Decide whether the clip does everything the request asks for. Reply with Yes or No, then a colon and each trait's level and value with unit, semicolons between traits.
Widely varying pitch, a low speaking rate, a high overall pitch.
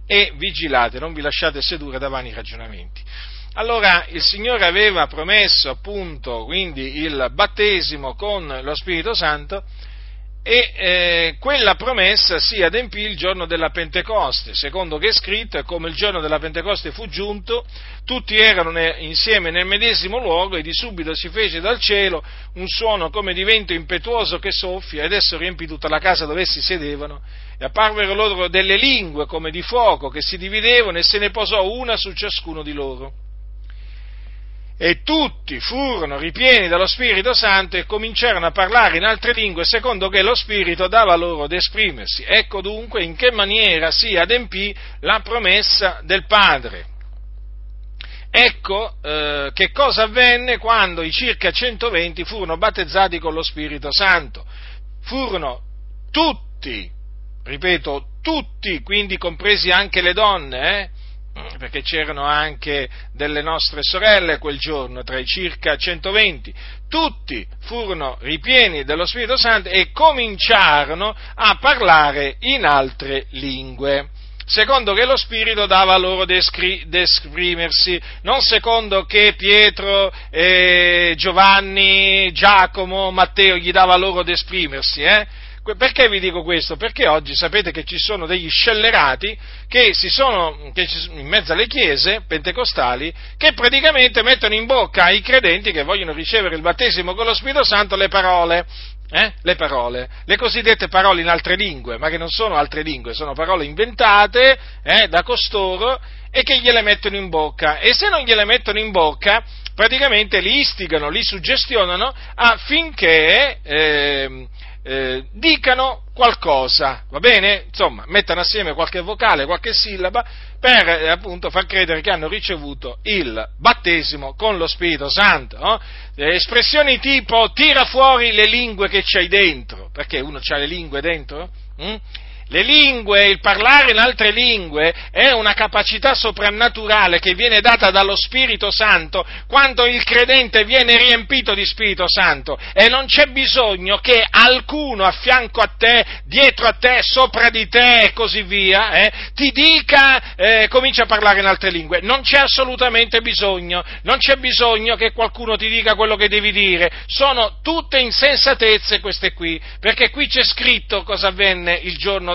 No: wide, 5.8 semitones; average, 150 wpm; high, 195 Hz